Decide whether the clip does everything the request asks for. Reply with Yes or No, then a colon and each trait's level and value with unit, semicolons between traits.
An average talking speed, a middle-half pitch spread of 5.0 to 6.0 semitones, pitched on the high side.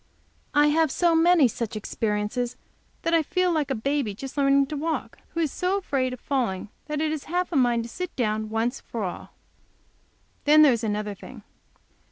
Yes: average, 195 wpm; wide, 5.6 semitones; very high, 275 Hz